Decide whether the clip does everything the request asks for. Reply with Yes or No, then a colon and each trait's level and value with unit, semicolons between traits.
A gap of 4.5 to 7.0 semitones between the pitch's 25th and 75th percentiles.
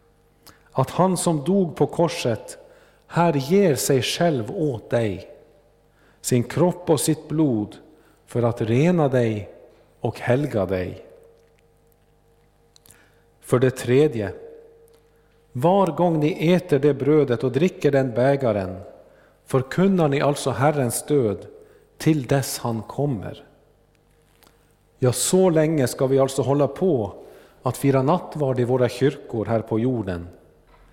Yes: average, 5.3 semitones